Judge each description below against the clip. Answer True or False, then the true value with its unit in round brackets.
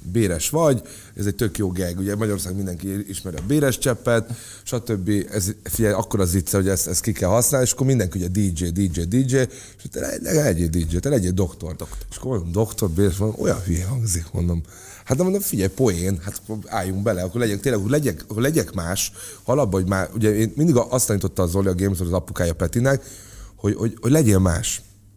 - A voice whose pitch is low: True (100 Hz)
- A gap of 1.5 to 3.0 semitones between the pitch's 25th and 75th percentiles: False (3.7 semitones)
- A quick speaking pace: True (210 wpm)